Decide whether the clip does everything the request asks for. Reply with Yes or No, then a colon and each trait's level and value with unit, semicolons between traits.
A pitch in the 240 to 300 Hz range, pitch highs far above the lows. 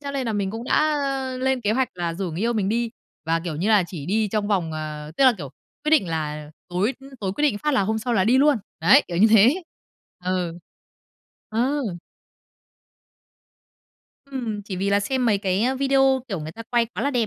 No: high, 215 Hz; wide, 5.9 semitones